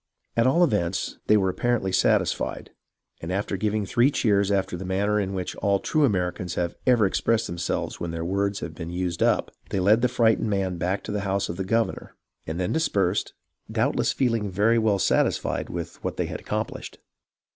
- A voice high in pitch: No, low, 100 Hz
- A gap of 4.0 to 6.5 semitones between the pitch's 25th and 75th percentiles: No, average, 3.3 semitones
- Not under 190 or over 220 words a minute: Yes, average, 195 wpm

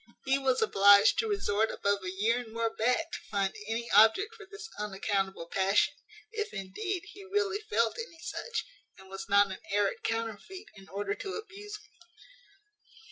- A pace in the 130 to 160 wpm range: No, average, 170 wpm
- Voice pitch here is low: No, high, 225 Hz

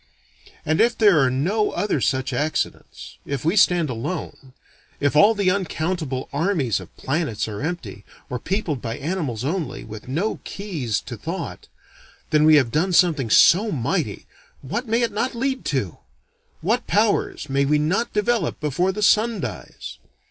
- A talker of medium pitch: Yes, medium, 155 Hz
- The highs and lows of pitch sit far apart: Yes, wide, 7.2 semitones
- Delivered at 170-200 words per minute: No, average, 160 wpm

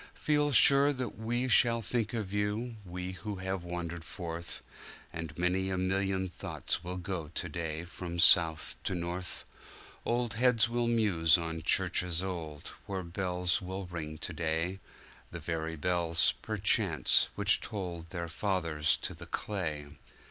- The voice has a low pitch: Yes, very low, 90 Hz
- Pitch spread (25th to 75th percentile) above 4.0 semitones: No, average, 3.5 semitones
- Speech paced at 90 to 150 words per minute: Yes, average, 140 wpm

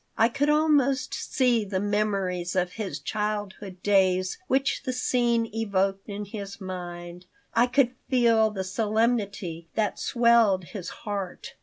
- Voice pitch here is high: Yes, high, 205 Hz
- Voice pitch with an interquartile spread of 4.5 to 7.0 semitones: No, average, 3.9 semitones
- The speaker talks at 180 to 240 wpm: No, slow, 135 wpm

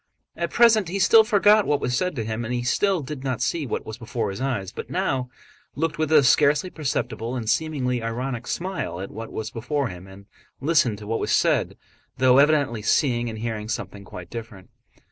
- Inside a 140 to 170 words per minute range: No, average, 200 wpm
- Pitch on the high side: No, low, 125 Hz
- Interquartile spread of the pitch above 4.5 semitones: Yes, average, 5.3 semitones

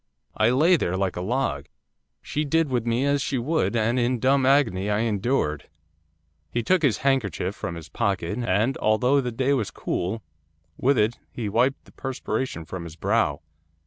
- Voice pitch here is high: No, low, 115 Hz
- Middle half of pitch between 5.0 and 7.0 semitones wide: Yes, average, 5.3 semitones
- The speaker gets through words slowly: No, average, 175 wpm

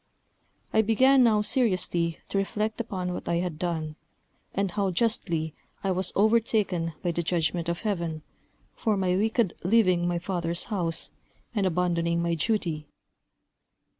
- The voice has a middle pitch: Yes, medium, 180 Hz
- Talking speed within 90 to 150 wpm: Yes, average, 140 wpm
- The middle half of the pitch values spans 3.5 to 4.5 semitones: Yes, average, 3.8 semitones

